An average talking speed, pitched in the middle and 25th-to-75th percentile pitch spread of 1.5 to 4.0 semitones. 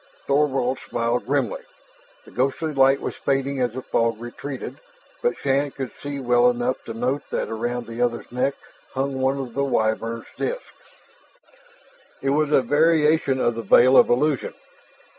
No: average, 160 wpm; low, 130 Hz; narrow, 2.5 semitones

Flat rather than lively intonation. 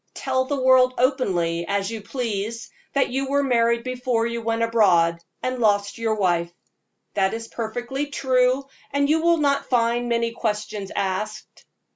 No: average, 3.7 semitones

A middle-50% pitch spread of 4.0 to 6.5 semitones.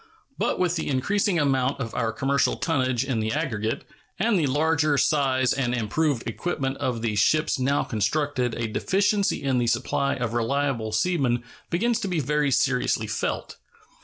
Yes: average, 4.4 semitones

